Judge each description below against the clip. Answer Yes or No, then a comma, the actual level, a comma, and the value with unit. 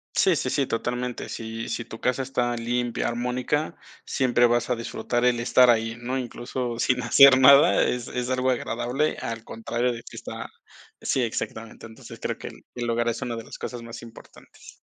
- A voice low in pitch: Yes, low, 120 Hz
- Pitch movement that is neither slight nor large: No, narrow, 1.4 semitones